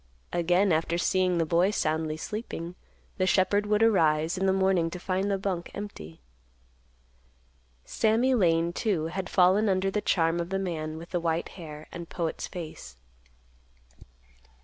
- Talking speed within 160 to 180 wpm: No, average, 150 wpm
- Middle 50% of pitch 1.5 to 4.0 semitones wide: Yes, average, 2.8 semitones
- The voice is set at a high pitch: No, medium, 180 Hz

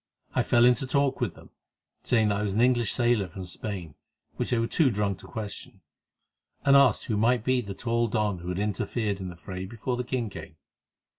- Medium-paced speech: No, fast, 215 wpm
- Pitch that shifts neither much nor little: Yes, average, 3.7 semitones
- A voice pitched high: No, low, 110 Hz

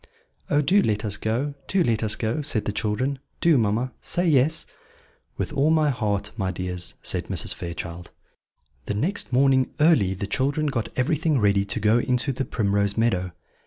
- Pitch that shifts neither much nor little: No, wide, 6.0 semitones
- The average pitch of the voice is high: No, low, 120 Hz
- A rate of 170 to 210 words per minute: Yes, average, 175 wpm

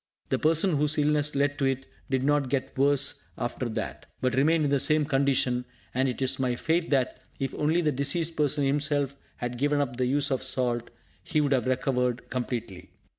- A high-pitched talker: No, medium, 140 Hz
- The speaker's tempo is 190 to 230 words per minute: Yes, average, 195 wpm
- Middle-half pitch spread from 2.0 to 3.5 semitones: Yes, narrow, 2.4 semitones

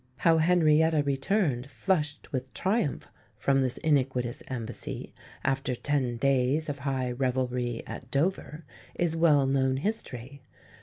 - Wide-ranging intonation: No, average, 3.6 semitones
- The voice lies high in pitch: No, medium, 140 Hz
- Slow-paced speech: Yes, slow, 120 wpm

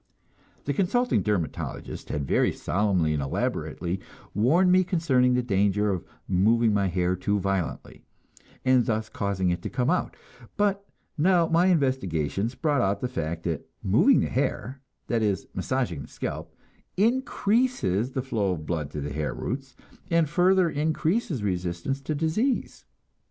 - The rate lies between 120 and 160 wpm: Yes, average, 150 wpm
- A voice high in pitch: No, low, 115 Hz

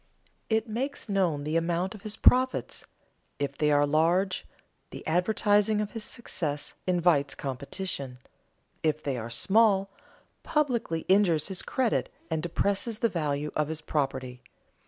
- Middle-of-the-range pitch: Yes, medium, 175 Hz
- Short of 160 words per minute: Yes, slow, 135 wpm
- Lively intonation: Yes, wide, 6.1 semitones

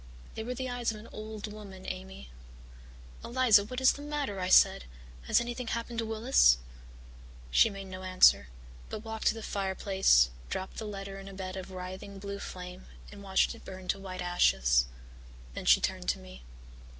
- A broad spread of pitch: No, average, 3.2 semitones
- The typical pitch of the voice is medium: No, high, 195 Hz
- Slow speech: No, average, 185 wpm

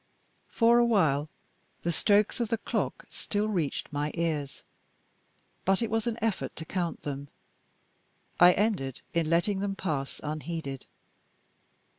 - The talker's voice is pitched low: No, medium, 175 Hz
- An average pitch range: No, wide, 5.9 semitones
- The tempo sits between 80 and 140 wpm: Yes, slow, 135 wpm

